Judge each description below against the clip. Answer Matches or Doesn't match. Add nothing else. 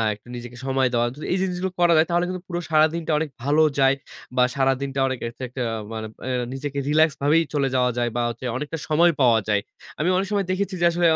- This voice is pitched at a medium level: Matches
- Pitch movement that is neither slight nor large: Matches